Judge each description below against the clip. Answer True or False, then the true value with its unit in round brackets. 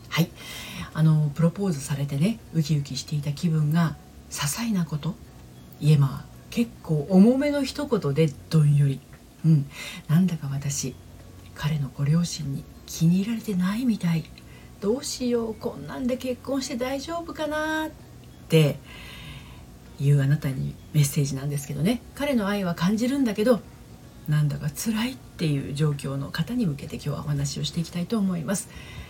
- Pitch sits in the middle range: True (160 Hz)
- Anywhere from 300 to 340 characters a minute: True (320 characters per minute)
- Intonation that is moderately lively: False (7.1 semitones)